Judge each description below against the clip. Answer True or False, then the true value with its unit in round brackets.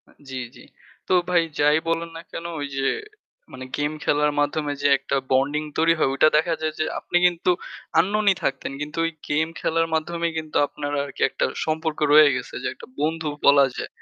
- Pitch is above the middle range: False (155 Hz)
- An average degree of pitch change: False (2.1 semitones)